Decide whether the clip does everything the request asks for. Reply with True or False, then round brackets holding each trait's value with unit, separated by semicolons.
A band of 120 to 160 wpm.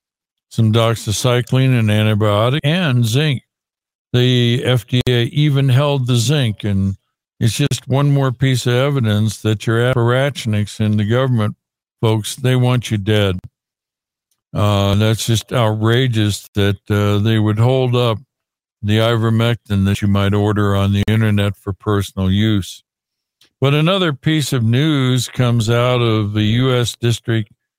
True (140 wpm)